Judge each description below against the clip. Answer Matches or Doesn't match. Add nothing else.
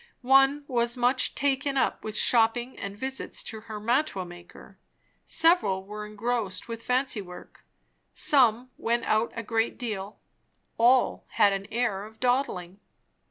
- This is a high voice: Matches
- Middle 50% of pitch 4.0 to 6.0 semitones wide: Doesn't match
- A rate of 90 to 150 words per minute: Matches